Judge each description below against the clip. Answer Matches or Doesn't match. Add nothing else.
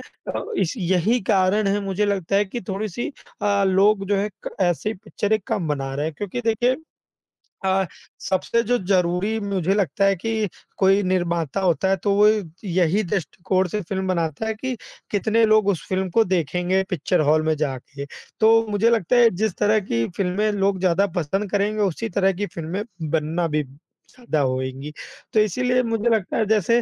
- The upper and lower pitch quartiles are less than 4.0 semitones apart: Matches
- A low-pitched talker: Doesn't match